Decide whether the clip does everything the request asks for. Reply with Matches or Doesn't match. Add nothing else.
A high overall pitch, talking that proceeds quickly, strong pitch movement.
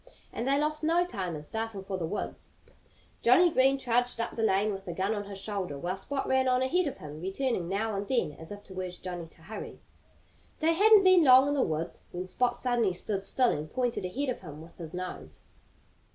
Matches